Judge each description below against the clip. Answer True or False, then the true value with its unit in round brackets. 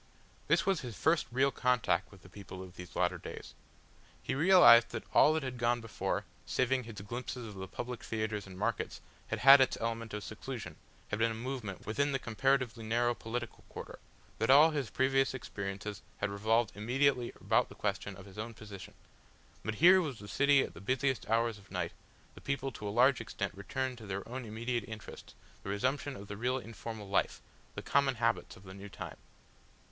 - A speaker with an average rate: True (195 wpm)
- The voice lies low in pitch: True (115 Hz)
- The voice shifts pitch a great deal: False (4.1 semitones)